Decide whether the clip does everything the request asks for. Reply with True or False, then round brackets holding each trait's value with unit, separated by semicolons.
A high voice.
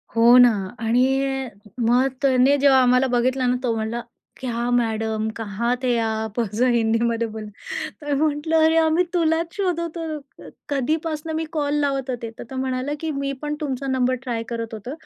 True (255 Hz)